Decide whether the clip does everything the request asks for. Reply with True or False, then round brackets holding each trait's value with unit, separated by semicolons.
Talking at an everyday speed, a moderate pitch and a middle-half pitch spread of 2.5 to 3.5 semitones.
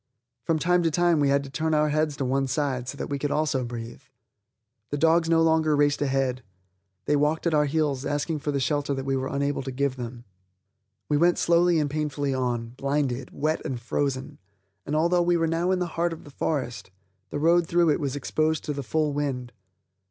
False (215 wpm; 145 Hz; 2.8 semitones)